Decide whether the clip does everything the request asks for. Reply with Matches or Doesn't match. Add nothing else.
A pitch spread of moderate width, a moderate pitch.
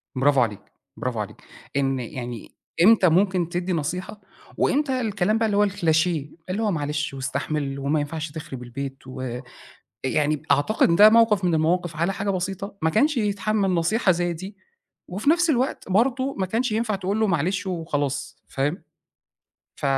Doesn't match